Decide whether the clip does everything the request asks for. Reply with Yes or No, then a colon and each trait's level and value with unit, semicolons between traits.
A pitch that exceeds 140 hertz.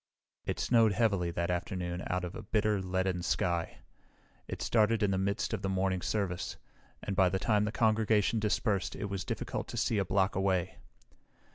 No: very low, 95 Hz